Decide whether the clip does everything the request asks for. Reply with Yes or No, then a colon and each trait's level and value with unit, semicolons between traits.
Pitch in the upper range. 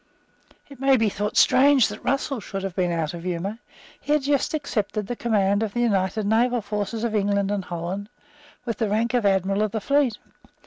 Yes: high, 210 Hz